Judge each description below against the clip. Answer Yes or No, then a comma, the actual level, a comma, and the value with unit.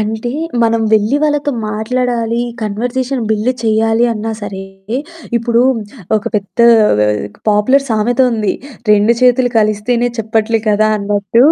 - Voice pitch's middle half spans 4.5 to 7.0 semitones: No, narrow, 2.4 semitones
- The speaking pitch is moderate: No, high, 225 Hz